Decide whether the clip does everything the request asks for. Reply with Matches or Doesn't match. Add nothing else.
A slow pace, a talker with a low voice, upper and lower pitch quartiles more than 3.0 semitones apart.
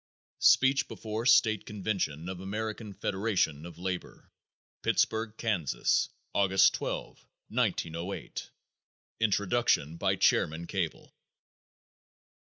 Matches